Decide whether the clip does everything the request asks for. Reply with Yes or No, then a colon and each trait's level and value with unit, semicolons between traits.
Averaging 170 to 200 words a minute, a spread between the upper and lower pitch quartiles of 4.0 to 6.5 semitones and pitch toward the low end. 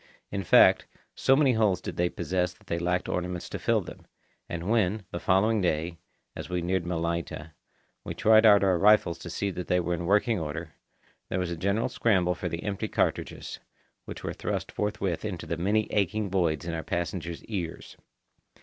No: average, 190 wpm; average, 3.1 semitones; very low, 90 Hz